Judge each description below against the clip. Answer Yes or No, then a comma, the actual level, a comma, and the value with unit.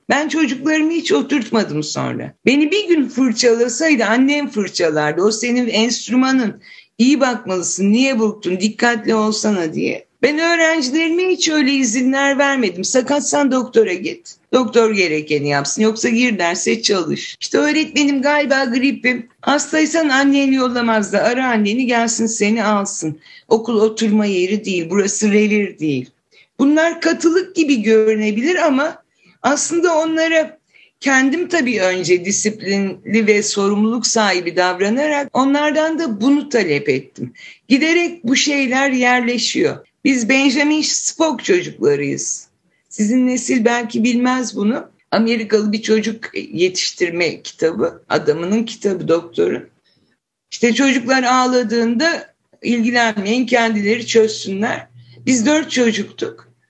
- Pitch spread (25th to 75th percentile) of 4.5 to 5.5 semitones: Yes, average, 5.1 semitones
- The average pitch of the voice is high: Yes, high, 240 Hz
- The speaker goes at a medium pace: Yes, average, 115 wpm